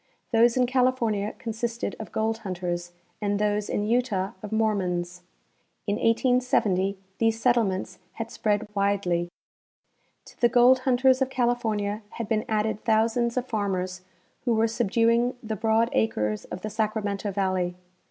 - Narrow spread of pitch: No, average, 3.0 semitones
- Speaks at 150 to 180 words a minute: No, average, 140 wpm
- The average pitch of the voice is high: Yes, high, 220 Hz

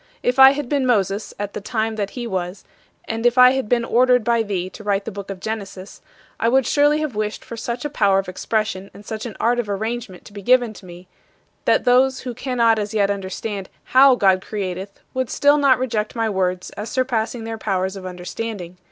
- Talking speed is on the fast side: Yes, fast, 215 wpm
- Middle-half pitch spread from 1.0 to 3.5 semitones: No, average, 3.9 semitones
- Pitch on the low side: No, high, 220 Hz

